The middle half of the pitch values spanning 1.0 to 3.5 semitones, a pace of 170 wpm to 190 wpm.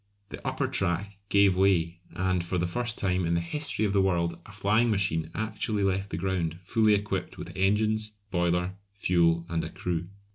Yes: average, 3.0 semitones; average, 185 wpm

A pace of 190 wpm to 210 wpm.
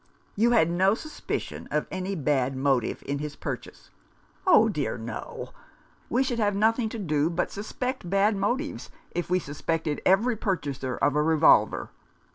No: average, 160 wpm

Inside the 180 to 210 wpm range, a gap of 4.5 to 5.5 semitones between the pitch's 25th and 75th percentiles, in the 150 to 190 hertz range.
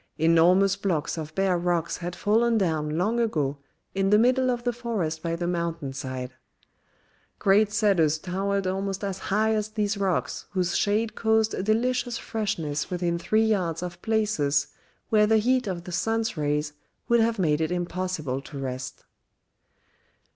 No: average, 160 wpm; average, 4.9 semitones; medium, 185 Hz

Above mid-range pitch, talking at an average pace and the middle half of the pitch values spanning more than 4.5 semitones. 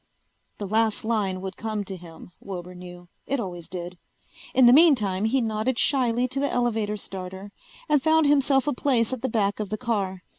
Yes: high, 215 Hz; average, 190 wpm; average, 5.0 semitones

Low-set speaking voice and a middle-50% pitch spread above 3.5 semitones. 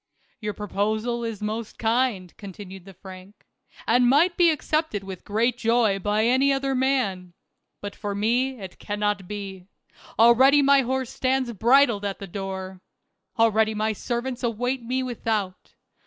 No: high, 220 Hz; average, 4.1 semitones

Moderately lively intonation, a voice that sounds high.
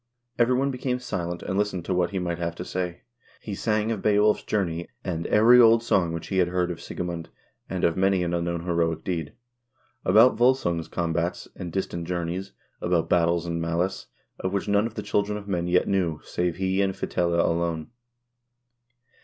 No: average, 3.1 semitones; very low, 90 Hz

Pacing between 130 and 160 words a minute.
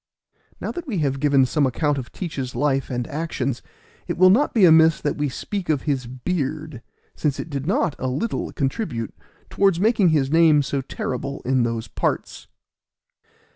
No: average, 175 wpm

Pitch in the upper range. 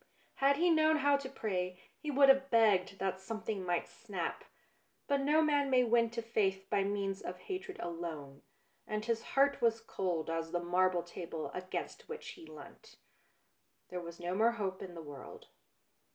Yes: high, 205 Hz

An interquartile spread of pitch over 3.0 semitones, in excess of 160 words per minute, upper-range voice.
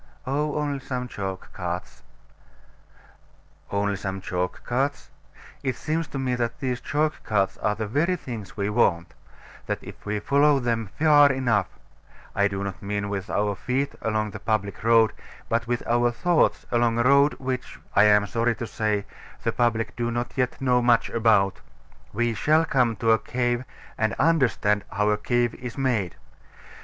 No: average, 3.9 semitones; average, 170 wpm; low, 115 Hz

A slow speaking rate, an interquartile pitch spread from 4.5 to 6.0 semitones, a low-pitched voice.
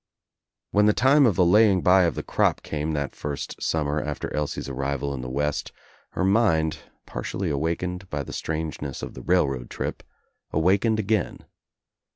No: average, 165 wpm; average, 4.8 semitones; very low, 80 Hz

